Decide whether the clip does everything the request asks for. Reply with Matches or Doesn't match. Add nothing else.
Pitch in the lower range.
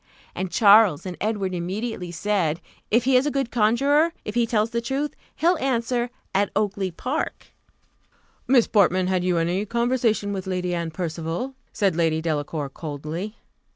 Doesn't match